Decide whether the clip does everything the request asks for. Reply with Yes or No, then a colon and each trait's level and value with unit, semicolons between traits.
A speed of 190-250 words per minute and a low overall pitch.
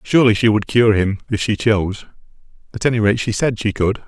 Yes: fast, 205 wpm; low, 110 Hz